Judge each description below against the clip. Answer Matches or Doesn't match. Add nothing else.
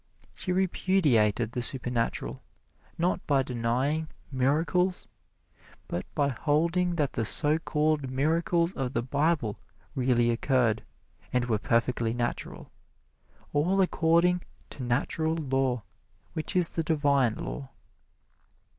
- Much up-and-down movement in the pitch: Doesn't match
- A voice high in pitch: Doesn't match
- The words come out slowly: Matches